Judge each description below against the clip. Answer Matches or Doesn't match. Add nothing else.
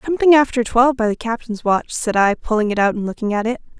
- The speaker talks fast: Matches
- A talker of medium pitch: Doesn't match